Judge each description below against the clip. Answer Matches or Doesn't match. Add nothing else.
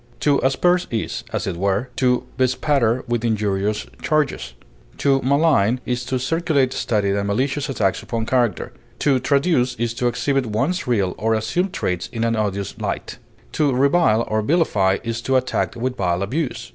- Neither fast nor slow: Matches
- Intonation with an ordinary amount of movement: Matches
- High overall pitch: Doesn't match